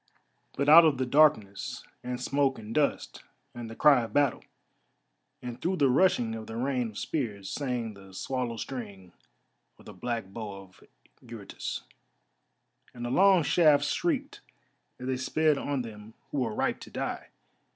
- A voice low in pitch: Yes, low, 125 Hz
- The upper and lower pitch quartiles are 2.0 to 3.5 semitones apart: No, average, 4.3 semitones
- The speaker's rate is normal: Yes, average, 160 wpm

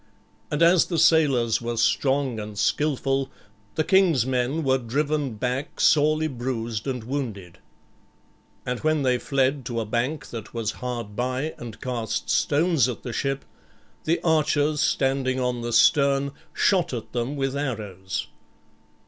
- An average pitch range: Yes, average, 3.8 semitones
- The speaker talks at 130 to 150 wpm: Yes, average, 145 wpm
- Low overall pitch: Yes, low, 130 Hz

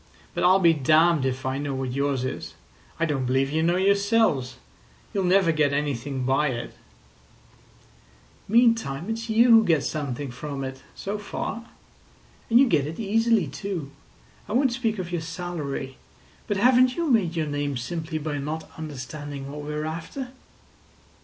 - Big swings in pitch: Yes, wide, 6.3 semitones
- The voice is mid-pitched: Yes, medium, 160 Hz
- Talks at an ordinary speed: Yes, average, 160 wpm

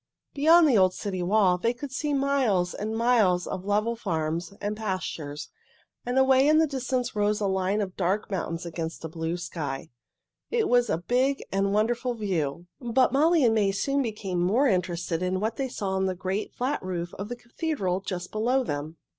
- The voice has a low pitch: No, high, 205 Hz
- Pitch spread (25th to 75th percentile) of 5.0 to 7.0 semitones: Yes, wide, 5.5 semitones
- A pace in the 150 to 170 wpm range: No, average, 190 wpm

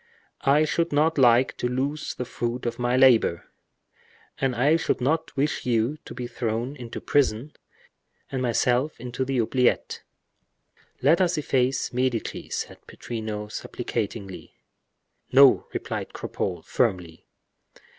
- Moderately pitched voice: No, low, 125 Hz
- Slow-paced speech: Yes, slow, 125 wpm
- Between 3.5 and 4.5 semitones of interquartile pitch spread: No, average, 3.0 semitones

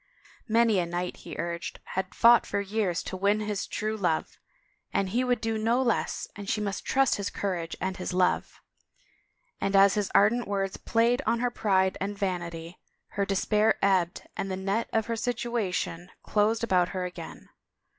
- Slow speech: No, average, 175 wpm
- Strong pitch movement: No, average, 3.3 semitones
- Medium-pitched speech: No, high, 200 Hz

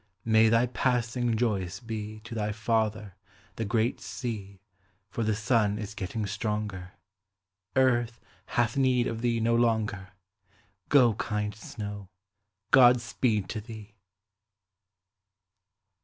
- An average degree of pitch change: No, narrow, 2.2 semitones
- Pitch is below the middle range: Yes, low, 110 Hz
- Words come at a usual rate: No, slow, 115 wpm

